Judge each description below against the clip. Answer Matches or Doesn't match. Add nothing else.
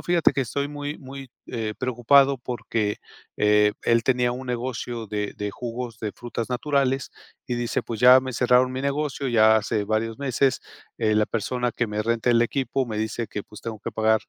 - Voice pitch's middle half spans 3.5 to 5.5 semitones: Doesn't match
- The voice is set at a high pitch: Doesn't match